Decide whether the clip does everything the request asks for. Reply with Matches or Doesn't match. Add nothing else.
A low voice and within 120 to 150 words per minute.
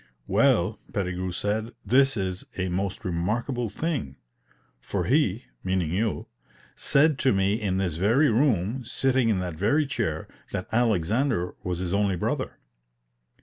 Matches